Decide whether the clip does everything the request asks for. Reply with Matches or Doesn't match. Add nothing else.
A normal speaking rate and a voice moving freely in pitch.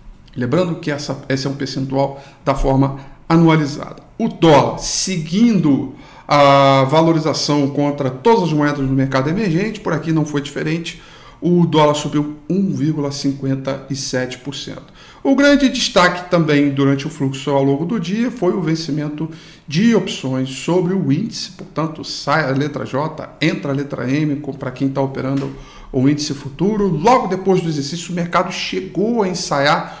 Doesn't match